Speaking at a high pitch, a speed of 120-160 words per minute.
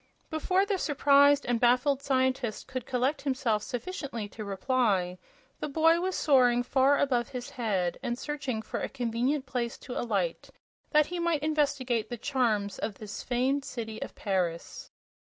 Yes: very high, 255 Hz; average, 155 wpm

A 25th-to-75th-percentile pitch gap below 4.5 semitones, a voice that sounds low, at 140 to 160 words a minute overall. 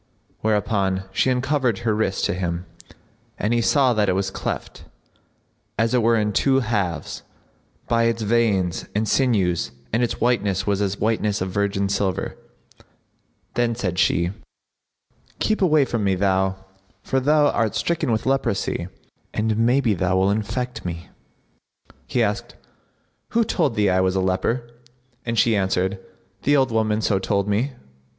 Yes: average, 3.9 semitones; low, 105 Hz; average, 155 wpm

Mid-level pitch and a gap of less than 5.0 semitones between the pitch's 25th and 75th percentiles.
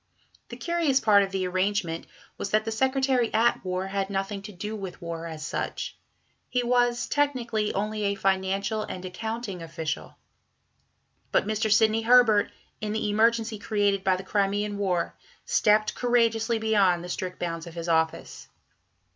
No: high, 205 Hz; average, 3.1 semitones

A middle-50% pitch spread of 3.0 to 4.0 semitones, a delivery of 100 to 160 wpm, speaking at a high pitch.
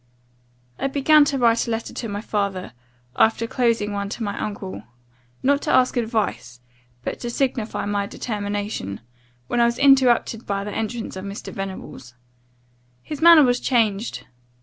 Yes: average, 3.6 semitones; average, 155 wpm; high, 225 Hz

